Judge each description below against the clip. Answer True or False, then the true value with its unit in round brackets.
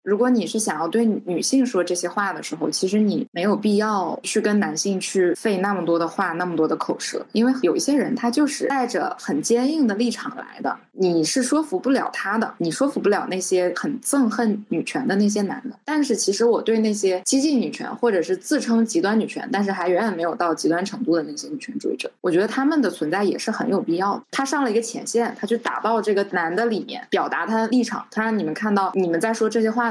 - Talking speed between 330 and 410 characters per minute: True (355 characters per minute)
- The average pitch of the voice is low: False (225 Hz)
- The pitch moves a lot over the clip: False (4.8 semitones)